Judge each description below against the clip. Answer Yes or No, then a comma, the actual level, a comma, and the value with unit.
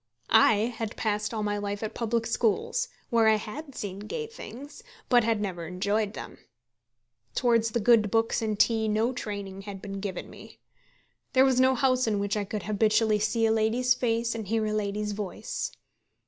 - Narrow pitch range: Yes, narrow, 2.1 semitones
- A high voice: Yes, high, 220 Hz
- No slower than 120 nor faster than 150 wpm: No, average, 185 wpm